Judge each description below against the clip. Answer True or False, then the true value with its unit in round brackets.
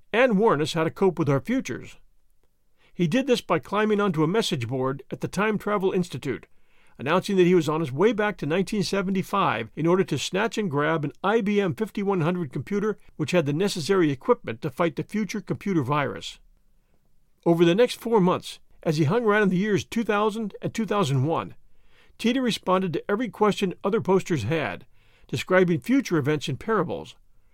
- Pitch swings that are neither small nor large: True (4.6 semitones)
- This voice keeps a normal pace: True (180 wpm)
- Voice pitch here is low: False (185 Hz)